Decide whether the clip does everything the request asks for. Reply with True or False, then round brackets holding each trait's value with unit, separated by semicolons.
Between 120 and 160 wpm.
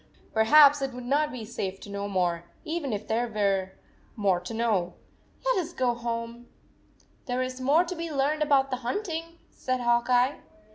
False (185 wpm)